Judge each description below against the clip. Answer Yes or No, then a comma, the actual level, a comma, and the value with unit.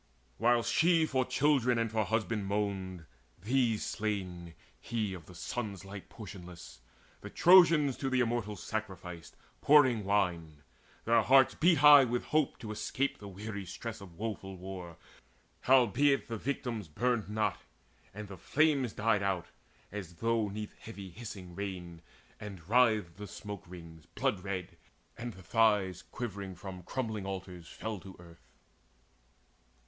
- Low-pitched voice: Yes, low, 105 Hz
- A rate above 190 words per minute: No, average, 145 wpm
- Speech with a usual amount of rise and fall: Yes, average, 4.3 semitones